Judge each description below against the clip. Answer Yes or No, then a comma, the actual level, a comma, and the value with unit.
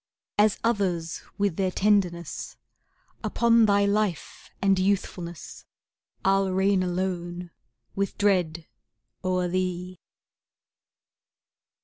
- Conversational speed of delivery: No, slow, 85 wpm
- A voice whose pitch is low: No, medium, 185 Hz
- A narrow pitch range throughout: Yes, narrow, 2.2 semitones